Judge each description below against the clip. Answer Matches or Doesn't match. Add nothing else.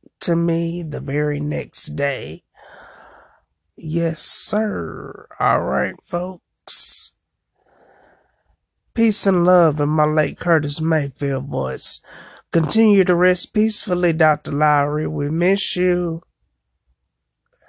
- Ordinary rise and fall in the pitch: Matches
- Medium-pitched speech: Matches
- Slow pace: Matches